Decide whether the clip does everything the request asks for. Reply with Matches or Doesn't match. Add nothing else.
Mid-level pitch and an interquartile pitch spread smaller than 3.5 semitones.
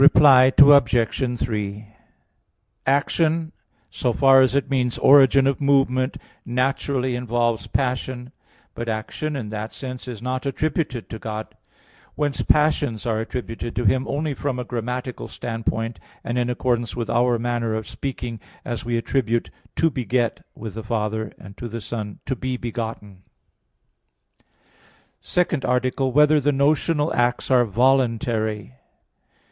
Doesn't match